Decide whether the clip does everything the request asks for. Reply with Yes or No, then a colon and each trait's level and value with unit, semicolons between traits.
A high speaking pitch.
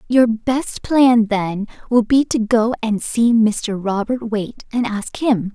Yes: high, 225 Hz